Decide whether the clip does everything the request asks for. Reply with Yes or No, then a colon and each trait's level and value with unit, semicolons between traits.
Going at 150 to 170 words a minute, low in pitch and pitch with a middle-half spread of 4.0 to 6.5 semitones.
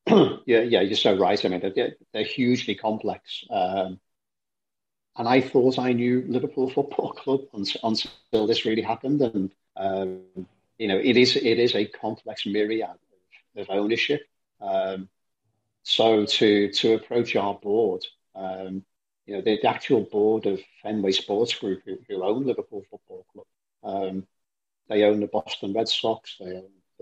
Yes: average, 160 wpm; low, 110 Hz; average, 4.8 semitones